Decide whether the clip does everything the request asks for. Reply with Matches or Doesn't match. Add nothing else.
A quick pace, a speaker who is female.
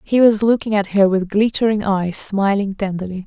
Doesn't match